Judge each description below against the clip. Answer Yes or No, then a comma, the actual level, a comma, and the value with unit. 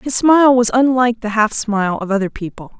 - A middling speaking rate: No, fast, 215 wpm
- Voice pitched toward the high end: Yes, high, 230 Hz